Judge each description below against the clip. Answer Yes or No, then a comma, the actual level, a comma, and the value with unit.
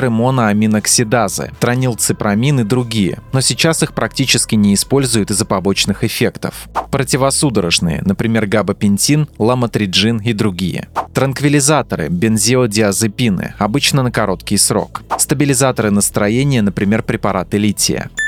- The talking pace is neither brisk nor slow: No, slow, 100 wpm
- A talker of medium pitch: No, low, 115 Hz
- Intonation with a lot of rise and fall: No, average, 4.2 semitones